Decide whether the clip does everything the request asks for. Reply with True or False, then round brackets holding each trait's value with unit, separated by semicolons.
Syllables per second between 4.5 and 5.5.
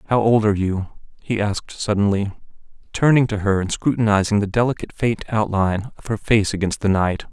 False (5.8 syllables/s)